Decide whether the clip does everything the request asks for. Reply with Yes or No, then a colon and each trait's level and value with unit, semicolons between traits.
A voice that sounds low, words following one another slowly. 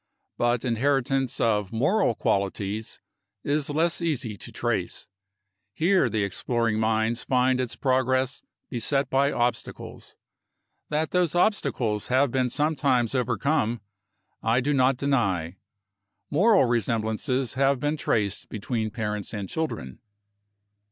Yes: low, 125 Hz; slow, 115 wpm